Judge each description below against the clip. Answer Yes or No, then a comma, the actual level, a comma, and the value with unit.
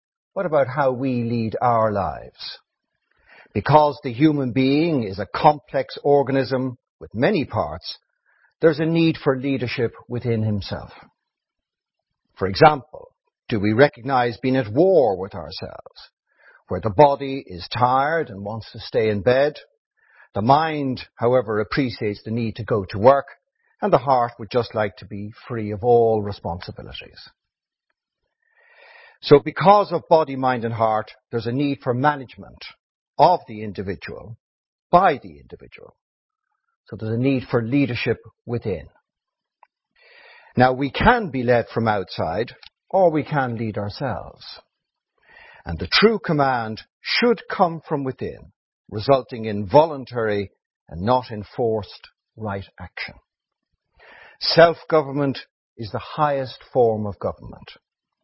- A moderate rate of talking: No, slow, 130 wpm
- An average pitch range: Yes, average, 4.9 semitones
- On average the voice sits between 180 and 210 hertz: No, low, 125 Hz